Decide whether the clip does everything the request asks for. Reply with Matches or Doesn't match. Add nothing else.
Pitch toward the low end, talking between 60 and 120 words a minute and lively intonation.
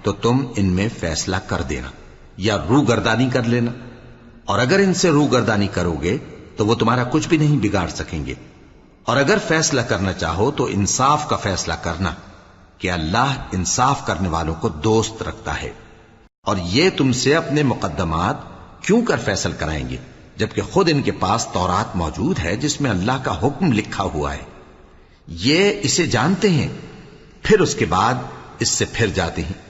Doesn't match